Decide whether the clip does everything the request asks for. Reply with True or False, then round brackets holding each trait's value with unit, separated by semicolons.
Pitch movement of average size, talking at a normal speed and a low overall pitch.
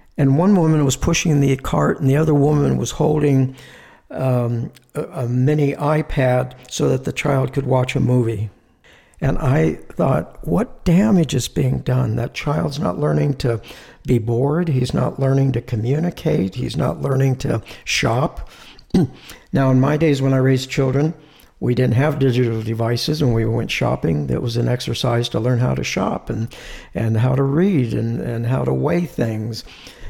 True (3.4 semitones; 175 wpm; 130 Hz)